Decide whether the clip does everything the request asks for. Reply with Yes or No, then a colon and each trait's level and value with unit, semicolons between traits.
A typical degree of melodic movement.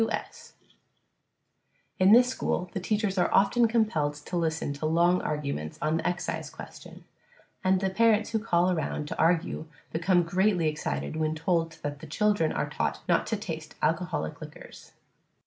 Yes: average, 3.8 semitones